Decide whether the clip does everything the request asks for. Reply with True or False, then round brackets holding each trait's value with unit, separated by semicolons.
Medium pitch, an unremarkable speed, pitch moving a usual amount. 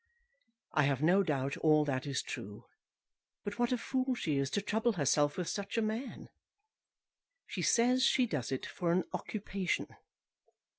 False (180 Hz; 160 wpm; 7.9 semitones)